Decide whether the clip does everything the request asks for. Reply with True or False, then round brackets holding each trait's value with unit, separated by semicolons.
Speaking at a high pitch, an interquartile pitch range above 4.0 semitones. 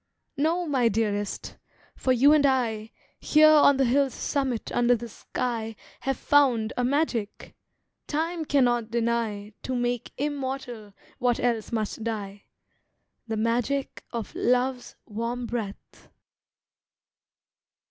False (245 Hz; 3.4 semitones)